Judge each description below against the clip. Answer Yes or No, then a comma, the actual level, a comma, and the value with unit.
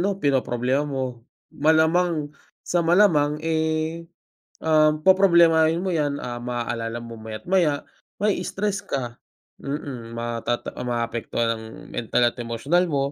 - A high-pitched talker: No, medium, 145 Hz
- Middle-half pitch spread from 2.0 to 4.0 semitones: No, wide, 5.5 semitones